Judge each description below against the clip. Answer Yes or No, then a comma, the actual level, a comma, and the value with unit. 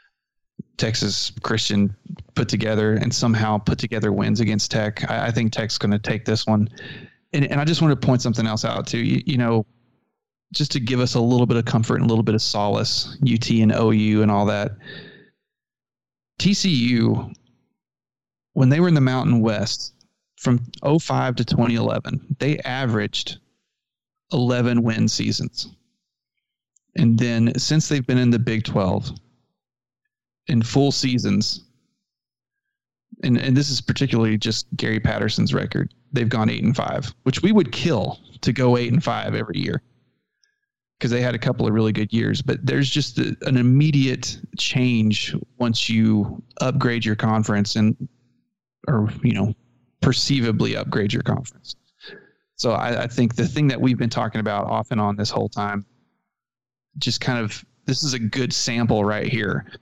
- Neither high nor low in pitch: No, low, 120 Hz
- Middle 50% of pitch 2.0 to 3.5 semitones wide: Yes, average, 3.1 semitones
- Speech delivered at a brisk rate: No, average, 165 wpm